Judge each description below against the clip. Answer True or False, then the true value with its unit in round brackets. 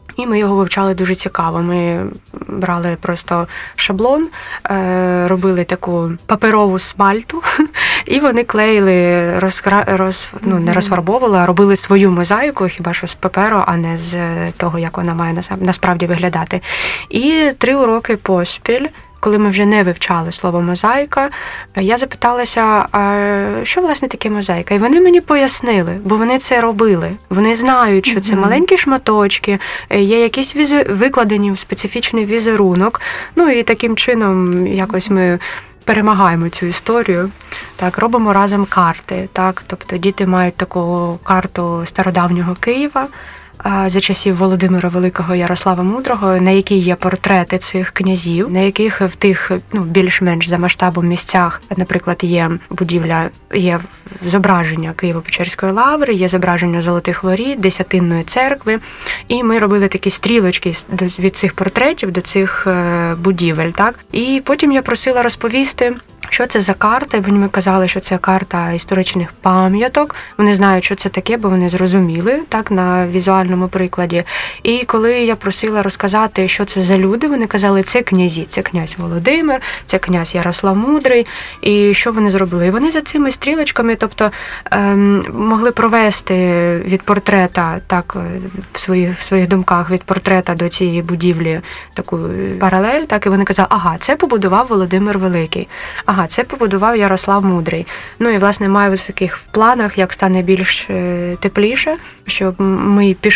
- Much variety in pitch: False (3.5 semitones)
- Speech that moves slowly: False (145 wpm)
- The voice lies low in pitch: False (195 Hz)